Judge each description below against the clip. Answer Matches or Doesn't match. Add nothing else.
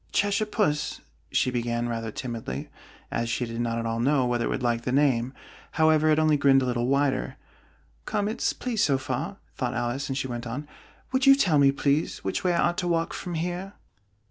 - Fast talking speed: Matches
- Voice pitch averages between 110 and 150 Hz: Matches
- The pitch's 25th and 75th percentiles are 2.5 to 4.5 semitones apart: Doesn't match